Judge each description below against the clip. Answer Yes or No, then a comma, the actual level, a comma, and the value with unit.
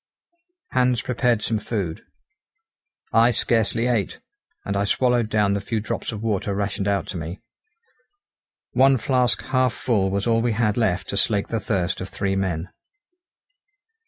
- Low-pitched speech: Yes, low, 105 Hz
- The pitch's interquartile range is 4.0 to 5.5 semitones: No, average, 3.2 semitones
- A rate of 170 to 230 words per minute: No, average, 155 wpm